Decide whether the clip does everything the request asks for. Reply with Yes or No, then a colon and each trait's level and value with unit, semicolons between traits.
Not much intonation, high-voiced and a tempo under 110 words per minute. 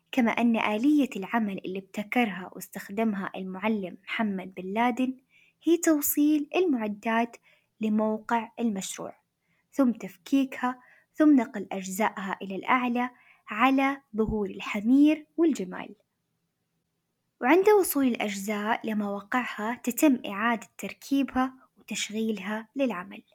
No: average, 4.2 semitones; high, 230 Hz; average, 95 wpm